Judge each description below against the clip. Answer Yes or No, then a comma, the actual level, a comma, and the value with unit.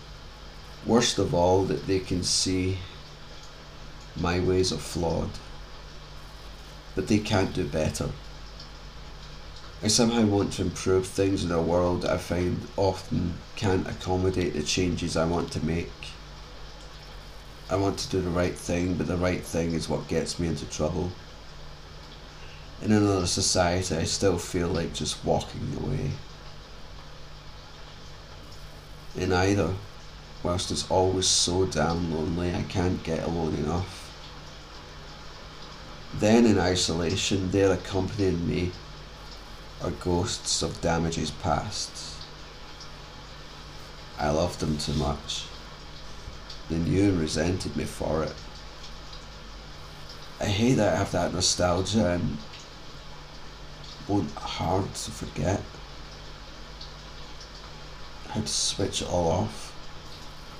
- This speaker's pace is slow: Yes, slow, 120 wpm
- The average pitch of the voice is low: Yes, very low, 85 Hz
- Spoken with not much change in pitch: No, average, 3.4 semitones